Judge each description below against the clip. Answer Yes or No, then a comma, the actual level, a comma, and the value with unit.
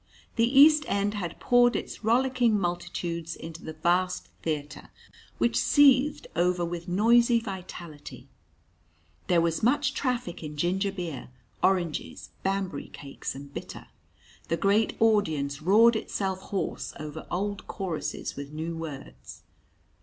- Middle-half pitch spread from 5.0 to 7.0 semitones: Yes, wide, 5.5 semitones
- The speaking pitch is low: No, medium, 180 Hz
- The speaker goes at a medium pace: No, slow, 125 wpm